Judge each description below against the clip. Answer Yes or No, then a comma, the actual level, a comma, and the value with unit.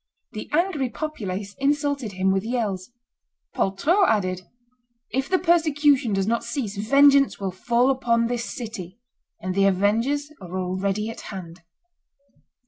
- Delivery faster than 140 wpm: No, slow, 135 wpm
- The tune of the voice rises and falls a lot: Yes, wide, 6.3 semitones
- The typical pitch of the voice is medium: No, high, 230 Hz